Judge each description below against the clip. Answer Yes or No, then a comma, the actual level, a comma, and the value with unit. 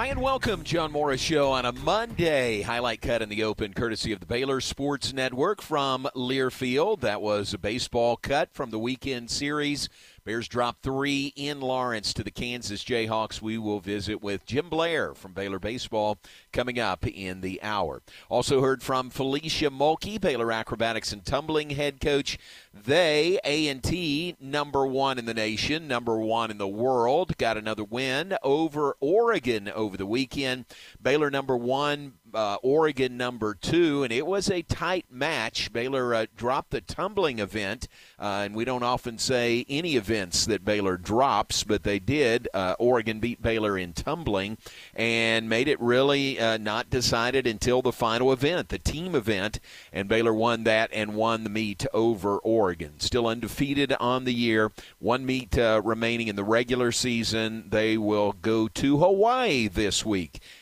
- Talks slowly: No, average, 165 wpm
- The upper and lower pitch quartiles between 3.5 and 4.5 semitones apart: Yes, average, 4.0 semitones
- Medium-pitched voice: No, low, 120 Hz